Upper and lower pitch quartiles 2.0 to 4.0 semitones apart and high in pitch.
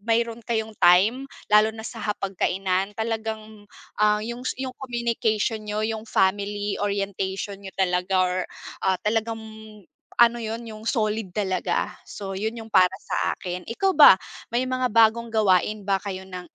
Yes: narrow, 2.6 semitones; high, 215 Hz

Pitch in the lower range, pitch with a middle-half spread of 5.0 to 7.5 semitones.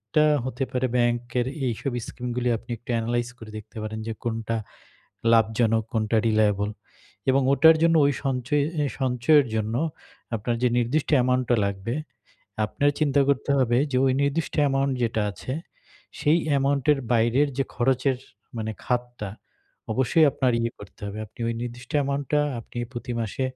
No: low, 125 Hz; average, 3.2 semitones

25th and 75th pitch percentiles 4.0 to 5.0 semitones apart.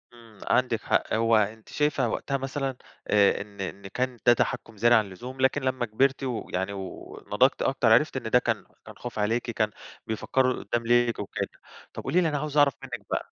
No: average, 3.6 semitones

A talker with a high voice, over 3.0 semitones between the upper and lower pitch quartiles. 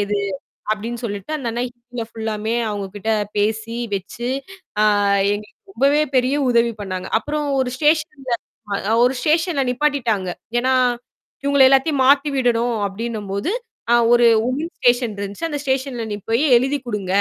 Yes: high, 240 Hz; average, 4.2 semitones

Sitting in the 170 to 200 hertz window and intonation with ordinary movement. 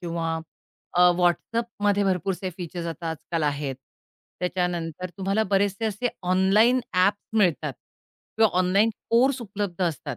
Yes: medium, 185 Hz; average, 3.3 semitones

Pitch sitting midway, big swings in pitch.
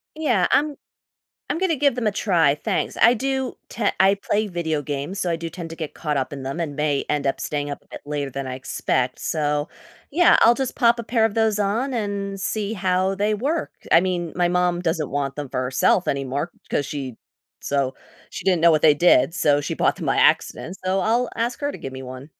Yes: medium, 175 Hz; wide, 6.9 semitones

